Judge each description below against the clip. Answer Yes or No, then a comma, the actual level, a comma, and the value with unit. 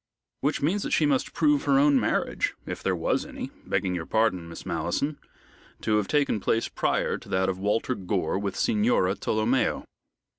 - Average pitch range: No, wide, 6.7 semitones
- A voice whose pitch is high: No, low, 110 Hz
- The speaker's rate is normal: Yes, average, 180 wpm